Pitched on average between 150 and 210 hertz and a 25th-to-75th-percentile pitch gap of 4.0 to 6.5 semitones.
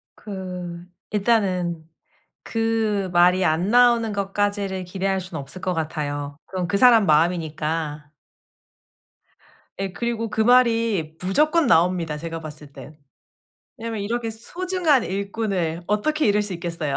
Yes: high, 190 Hz; average, 5.1 semitones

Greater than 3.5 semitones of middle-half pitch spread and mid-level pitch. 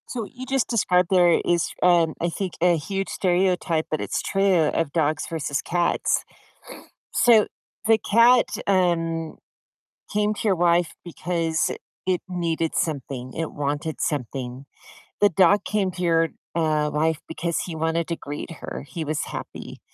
No: average, 2.9 semitones; medium, 170 Hz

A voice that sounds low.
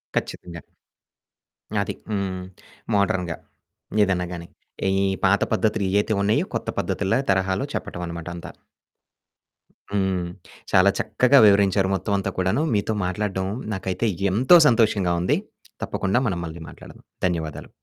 Yes: very low, 95 Hz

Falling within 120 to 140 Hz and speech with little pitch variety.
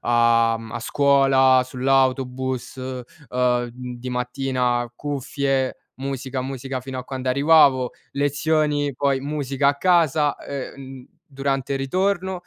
Yes: low, 135 Hz; narrow, 1.8 semitones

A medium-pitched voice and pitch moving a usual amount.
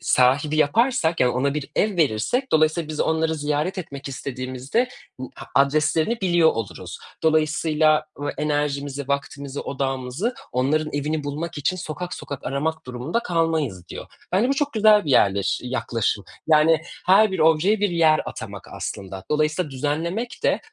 Yes: medium, 155 Hz; average, 3.5 semitones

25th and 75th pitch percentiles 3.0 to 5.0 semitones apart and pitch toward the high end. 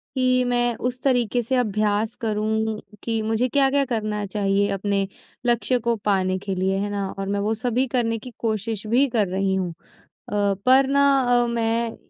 Yes: average, 3.3 semitones; high, 220 Hz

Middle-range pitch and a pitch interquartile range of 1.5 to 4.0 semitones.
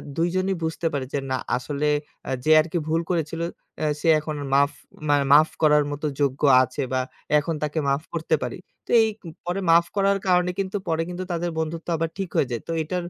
Yes: medium, 160 Hz; average, 3.2 semitones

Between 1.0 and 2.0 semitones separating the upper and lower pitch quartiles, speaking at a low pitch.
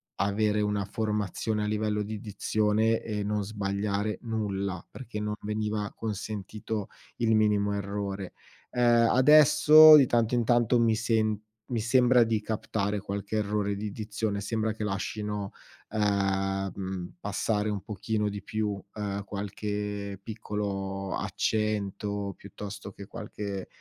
Yes: narrow, 1.5 semitones; low, 105 Hz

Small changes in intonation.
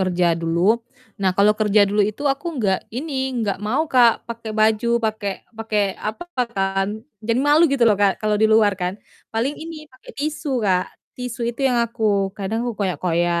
No: average, 3.7 semitones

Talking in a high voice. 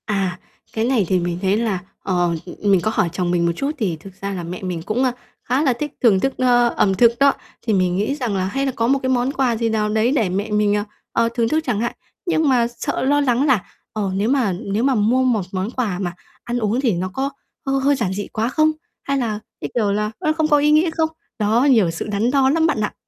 Yes: high, 225 Hz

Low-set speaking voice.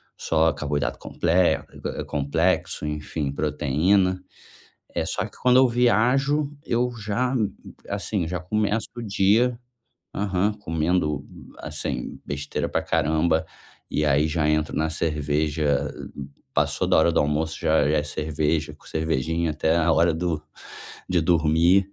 Yes: very low, 80 Hz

